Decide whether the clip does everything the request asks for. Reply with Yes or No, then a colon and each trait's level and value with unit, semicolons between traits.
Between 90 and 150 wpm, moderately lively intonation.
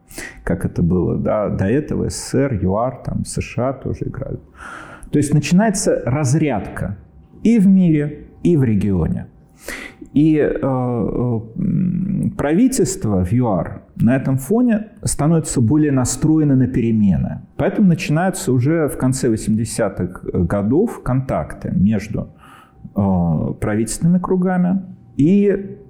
No: average, 115 wpm; wide, 7.3 semitones